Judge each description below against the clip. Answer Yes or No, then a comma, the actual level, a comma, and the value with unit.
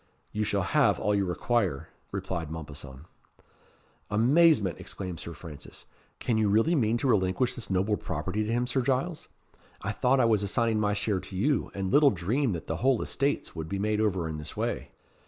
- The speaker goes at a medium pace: Yes, average, 190 wpm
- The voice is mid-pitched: No, low, 105 Hz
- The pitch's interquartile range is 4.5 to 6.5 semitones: Yes, average, 5.0 semitones